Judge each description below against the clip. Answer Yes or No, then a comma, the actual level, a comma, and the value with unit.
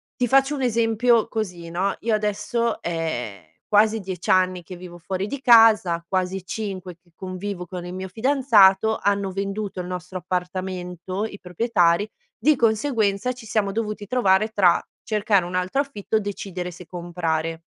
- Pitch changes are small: No, average, 3.6 semitones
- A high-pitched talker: Yes, high, 195 Hz